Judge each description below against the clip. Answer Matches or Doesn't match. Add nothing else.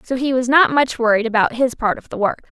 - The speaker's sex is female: Matches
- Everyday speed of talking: Doesn't match